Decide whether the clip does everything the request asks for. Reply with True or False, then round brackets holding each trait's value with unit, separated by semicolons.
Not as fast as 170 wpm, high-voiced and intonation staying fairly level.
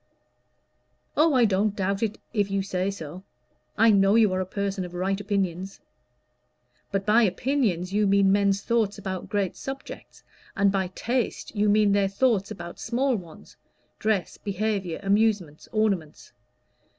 True (150 wpm; 200 Hz; 2.2 semitones)